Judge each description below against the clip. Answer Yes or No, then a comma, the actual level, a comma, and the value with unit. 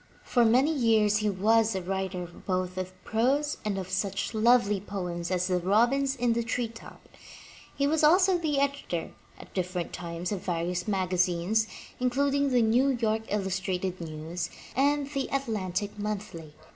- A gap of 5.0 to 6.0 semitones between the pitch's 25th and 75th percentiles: Yes, average, 5.3 semitones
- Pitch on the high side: Yes, high, 210 Hz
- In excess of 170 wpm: No, average, 155 wpm